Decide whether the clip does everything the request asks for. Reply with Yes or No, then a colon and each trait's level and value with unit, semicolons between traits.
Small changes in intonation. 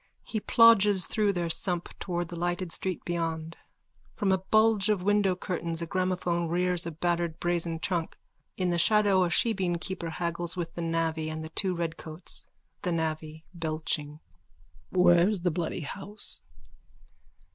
Yes: narrow, 2.3 semitones